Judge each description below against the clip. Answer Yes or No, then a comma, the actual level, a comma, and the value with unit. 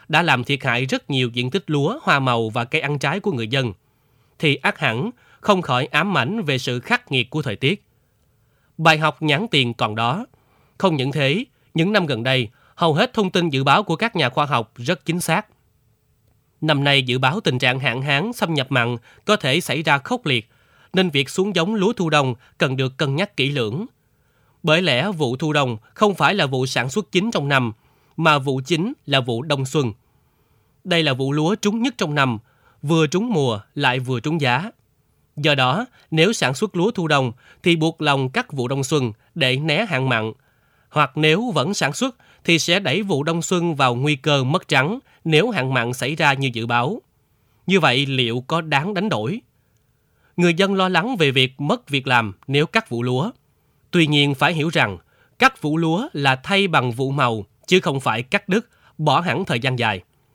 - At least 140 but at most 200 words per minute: No, average, 210 wpm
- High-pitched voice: No, medium, 145 Hz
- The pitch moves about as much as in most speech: Yes, average, 4.9 semitones